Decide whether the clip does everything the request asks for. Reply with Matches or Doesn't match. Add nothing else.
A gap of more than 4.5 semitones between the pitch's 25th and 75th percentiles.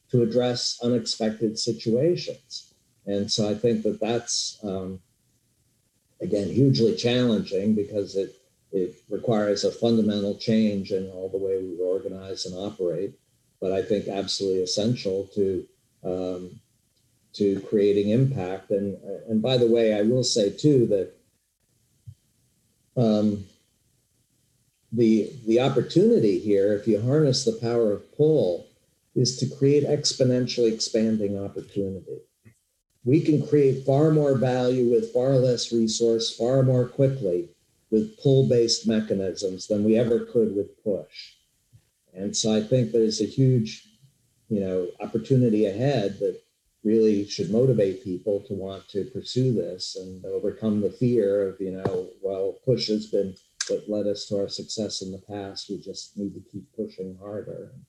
Doesn't match